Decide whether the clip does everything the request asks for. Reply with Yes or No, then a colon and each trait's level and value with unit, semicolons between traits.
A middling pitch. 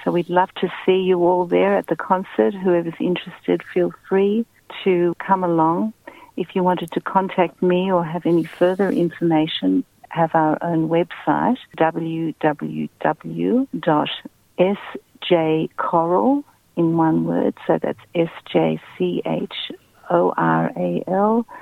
Yes: medium, 175 Hz